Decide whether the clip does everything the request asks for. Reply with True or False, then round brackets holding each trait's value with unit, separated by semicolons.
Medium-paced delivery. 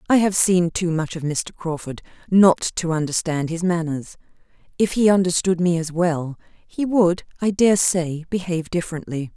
True (165 wpm)